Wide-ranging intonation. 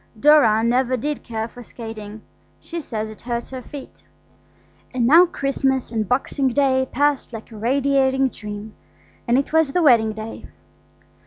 No: average, 3.7 semitones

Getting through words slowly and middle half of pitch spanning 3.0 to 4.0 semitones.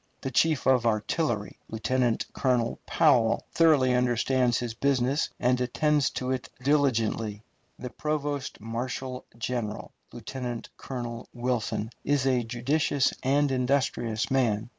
No: slow, 120 wpm; narrow, 2.5 semitones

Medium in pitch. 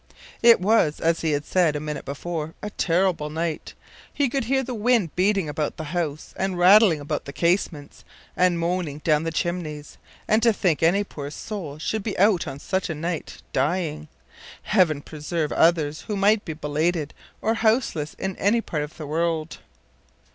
Yes: medium, 170 Hz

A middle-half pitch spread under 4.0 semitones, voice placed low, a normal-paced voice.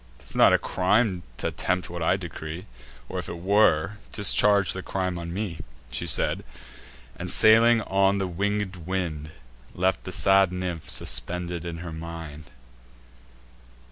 Yes: narrow, 2.5 semitones; very low, 90 Hz; average, 145 wpm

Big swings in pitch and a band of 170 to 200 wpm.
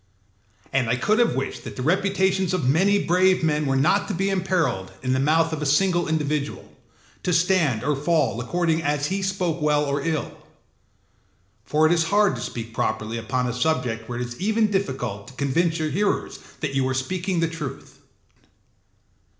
Yes: wide, 5.7 semitones; average, 185 wpm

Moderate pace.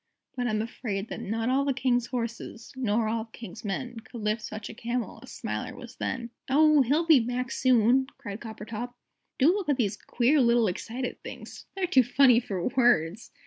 Yes: average, 190 wpm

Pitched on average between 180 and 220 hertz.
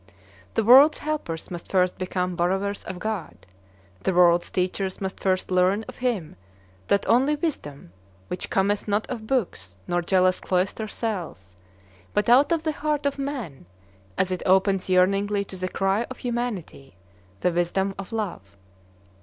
Yes: high, 190 Hz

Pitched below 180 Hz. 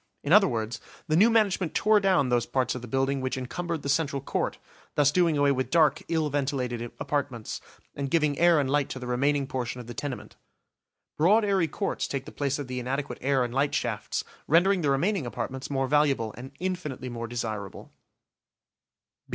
Yes: medium, 140 Hz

